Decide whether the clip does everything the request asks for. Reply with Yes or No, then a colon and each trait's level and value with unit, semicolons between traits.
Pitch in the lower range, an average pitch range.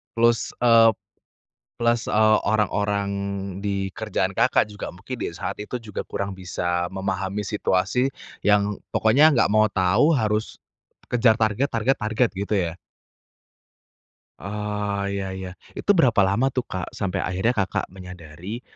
Yes: low, 105 Hz; average, 3.1 semitones